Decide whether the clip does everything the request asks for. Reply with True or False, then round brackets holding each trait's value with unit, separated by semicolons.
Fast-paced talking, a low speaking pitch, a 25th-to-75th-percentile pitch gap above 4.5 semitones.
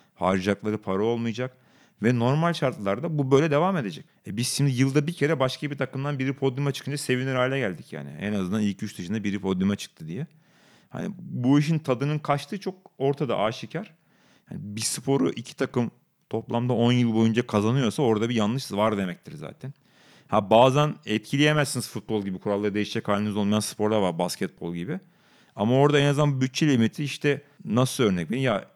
True (175 wpm; 125 Hz; 5.2 semitones)